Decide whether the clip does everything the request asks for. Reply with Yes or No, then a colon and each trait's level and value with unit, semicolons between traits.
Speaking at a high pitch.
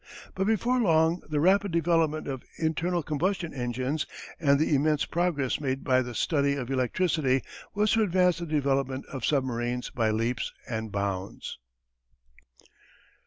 No: medium, 145 Hz